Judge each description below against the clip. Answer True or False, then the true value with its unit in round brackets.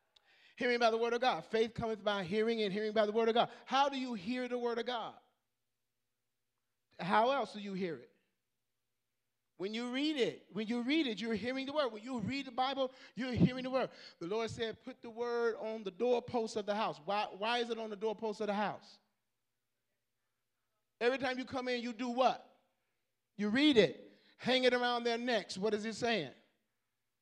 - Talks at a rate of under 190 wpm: False (205 wpm)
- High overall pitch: True (225 Hz)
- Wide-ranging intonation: True (5.9 semitones)